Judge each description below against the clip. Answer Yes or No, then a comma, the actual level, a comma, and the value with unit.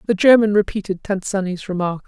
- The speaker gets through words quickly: No, average, 175 wpm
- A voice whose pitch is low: No, high, 200 Hz